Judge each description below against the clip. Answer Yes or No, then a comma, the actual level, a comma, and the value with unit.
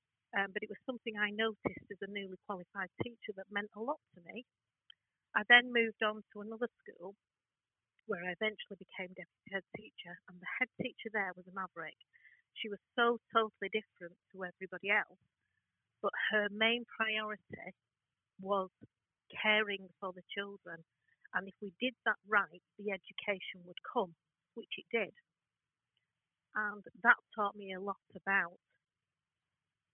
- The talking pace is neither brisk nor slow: Yes, average, 155 wpm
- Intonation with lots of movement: No, average, 2.9 semitones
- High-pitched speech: Yes, high, 200 Hz